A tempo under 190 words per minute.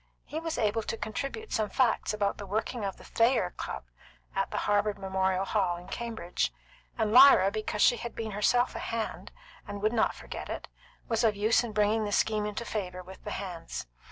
No: average, 200 wpm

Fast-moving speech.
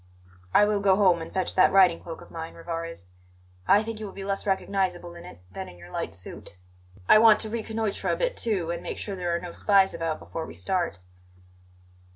Yes: fast, 215 wpm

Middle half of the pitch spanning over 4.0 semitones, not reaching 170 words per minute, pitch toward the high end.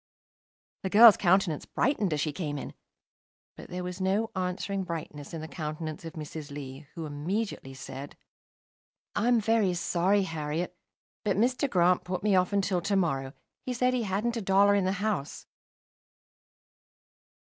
No: average, 4.6 semitones; average, 155 wpm; medium, 180 Hz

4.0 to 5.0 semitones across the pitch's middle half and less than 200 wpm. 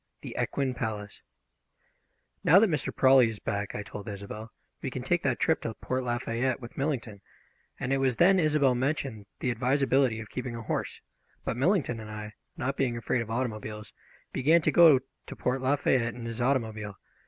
No: average, 3.4 semitones; average, 180 wpm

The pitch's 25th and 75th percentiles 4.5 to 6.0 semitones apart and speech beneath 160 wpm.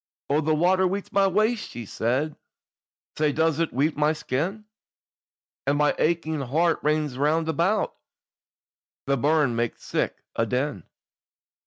No: average, 3.2 semitones; average, 140 wpm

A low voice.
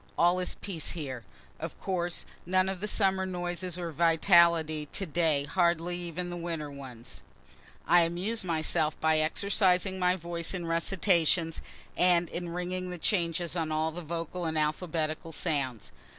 No: medium, 170 Hz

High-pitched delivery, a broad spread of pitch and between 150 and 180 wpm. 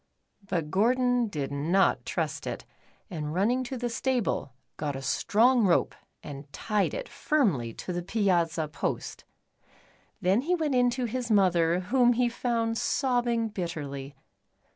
No: high, 210 Hz; wide, 6.9 semitones; average, 140 wpm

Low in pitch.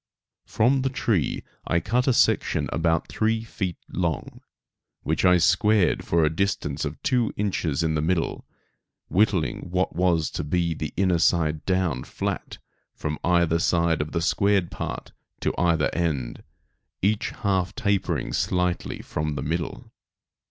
Yes: very low, 85 Hz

